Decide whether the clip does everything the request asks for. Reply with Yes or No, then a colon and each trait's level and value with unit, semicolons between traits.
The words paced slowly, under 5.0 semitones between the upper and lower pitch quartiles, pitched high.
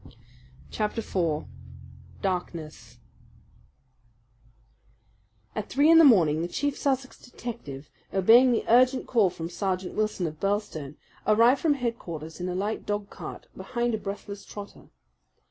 No: slow, 130 wpm; average, 5.3 semitones; high, 205 Hz